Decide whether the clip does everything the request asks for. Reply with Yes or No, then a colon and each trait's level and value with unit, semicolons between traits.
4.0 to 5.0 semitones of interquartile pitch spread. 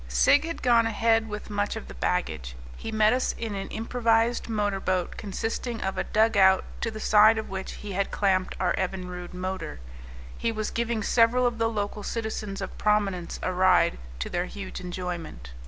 No: average, 3.3 semitones